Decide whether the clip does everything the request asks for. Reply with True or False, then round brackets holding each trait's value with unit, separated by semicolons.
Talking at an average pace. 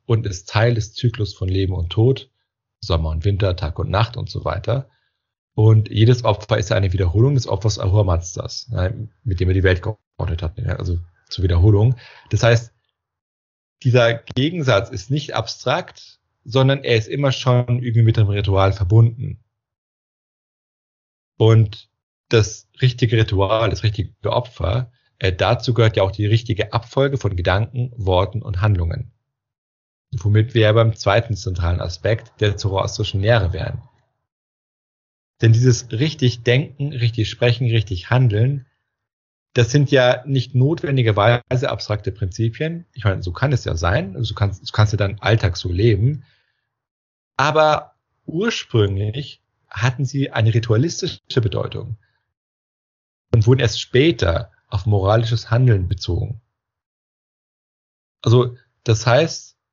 True (135 wpm)